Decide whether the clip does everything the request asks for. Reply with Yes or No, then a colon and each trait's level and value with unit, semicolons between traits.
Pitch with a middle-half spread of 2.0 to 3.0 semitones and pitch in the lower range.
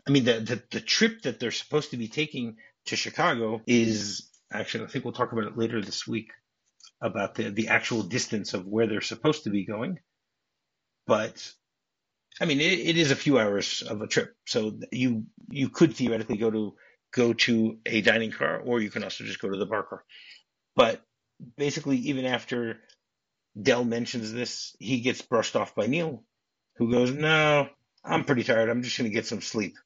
No: average, 3.7 semitones; low, 120 Hz